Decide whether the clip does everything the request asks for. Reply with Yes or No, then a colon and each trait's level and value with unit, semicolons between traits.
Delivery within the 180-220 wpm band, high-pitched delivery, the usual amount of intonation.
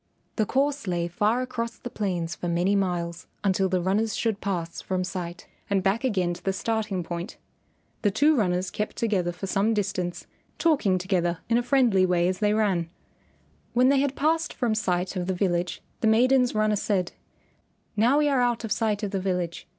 Yes: average, 190 wpm; high, 200 Hz; average, 4.2 semitones